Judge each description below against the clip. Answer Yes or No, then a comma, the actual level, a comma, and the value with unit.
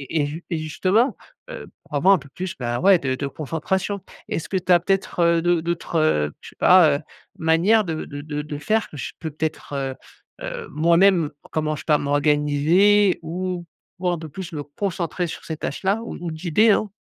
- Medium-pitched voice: Yes, medium, 165 Hz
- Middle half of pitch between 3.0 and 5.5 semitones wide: Yes, average, 3.9 semitones